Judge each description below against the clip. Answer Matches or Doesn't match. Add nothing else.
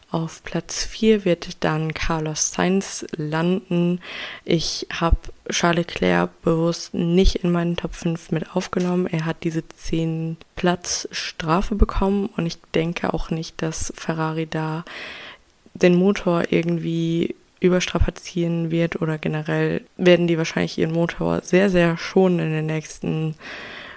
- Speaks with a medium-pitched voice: Matches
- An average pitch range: Doesn't match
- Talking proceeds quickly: Doesn't match